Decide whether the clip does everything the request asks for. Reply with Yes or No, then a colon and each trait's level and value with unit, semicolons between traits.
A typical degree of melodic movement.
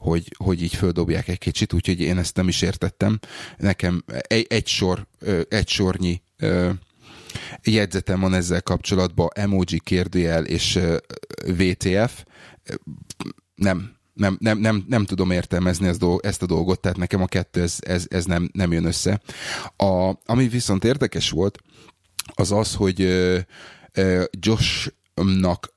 No: narrow, 2.1 semitones